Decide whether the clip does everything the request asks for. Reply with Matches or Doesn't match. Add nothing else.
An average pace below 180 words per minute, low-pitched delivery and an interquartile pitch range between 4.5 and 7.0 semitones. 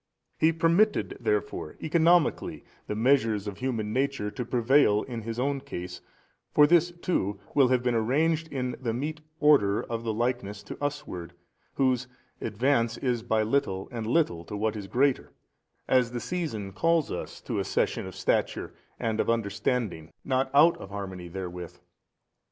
Matches